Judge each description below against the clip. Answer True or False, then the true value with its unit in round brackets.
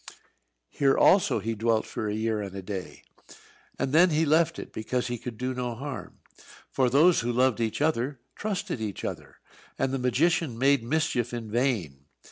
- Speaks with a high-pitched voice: False (125 Hz)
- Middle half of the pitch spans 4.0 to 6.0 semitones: True (4.5 semitones)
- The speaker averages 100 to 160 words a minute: False (180 wpm)